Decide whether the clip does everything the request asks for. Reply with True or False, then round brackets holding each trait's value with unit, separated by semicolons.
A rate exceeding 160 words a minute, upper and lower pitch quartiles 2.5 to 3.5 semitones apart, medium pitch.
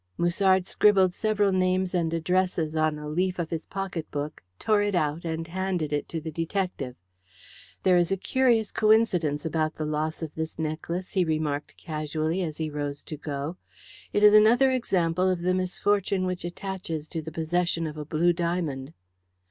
True (175 wpm; 3.2 semitones; 170 Hz)